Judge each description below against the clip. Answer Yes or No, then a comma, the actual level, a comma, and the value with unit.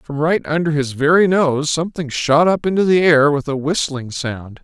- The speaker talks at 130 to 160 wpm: No, fast, 205 wpm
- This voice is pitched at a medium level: Yes, medium, 150 Hz